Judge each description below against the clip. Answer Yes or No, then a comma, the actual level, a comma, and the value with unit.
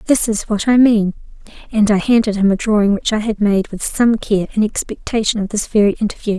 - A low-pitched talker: No, high, 210 Hz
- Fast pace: Yes, fast, 225 wpm